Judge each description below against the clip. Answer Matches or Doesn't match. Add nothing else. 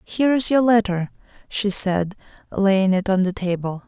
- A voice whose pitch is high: Matches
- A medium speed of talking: Matches